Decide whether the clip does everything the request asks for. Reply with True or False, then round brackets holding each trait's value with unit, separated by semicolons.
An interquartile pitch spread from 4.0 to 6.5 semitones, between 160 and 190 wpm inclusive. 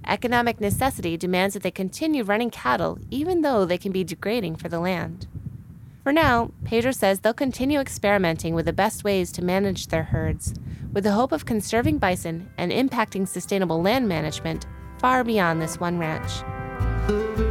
True (5.3 semitones; 165 wpm)